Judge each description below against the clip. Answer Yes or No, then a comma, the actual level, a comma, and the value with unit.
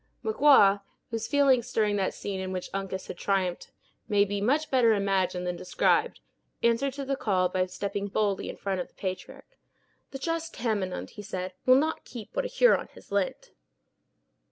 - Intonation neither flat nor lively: No, wide, 5.7 semitones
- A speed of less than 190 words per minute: Yes, average, 180 wpm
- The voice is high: Yes, high, 205 Hz